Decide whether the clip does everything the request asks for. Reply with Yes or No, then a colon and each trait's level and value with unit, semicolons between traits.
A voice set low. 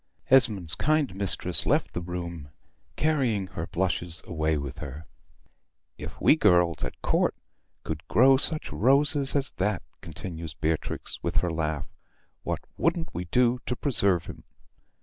Yes: very low, 90 Hz